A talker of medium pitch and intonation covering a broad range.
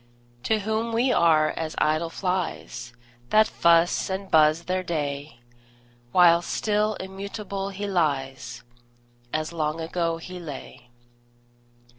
No: medium, 170 Hz; average, 4.1 semitones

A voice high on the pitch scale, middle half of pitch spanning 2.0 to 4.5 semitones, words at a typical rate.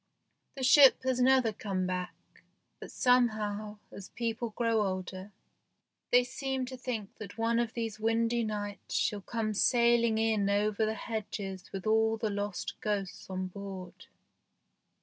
Yes: high, 220 Hz; average, 2.7 semitones; average, 145 wpm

